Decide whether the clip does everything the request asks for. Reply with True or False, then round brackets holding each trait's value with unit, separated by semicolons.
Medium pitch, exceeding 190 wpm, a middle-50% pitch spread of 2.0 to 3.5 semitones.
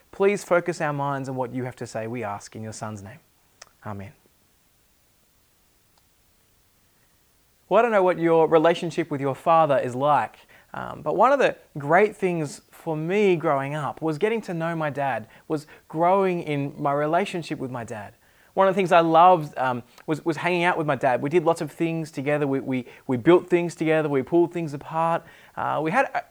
False (155 Hz; 200 wpm; 4.2 semitones)